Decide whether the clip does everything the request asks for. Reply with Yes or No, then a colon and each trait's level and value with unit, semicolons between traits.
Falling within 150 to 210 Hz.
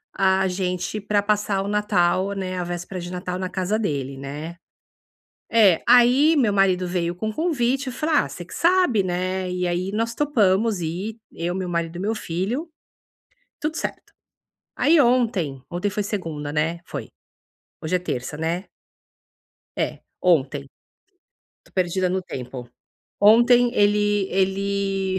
Yes: high, 190 Hz